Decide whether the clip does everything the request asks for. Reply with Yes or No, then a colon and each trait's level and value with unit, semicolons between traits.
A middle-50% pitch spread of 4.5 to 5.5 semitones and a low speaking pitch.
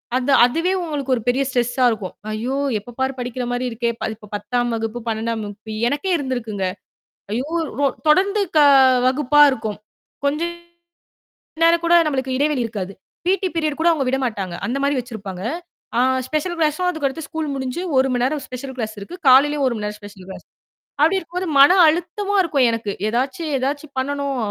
No: average, 4.8 semitones; very high, 265 Hz